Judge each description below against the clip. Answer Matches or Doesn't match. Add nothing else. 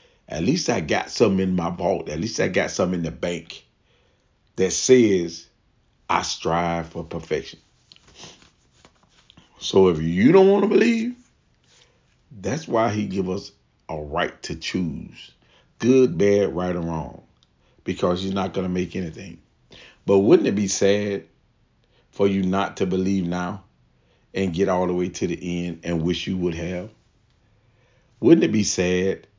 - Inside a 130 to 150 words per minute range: Doesn't match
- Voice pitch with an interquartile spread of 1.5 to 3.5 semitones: Matches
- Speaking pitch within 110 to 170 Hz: Doesn't match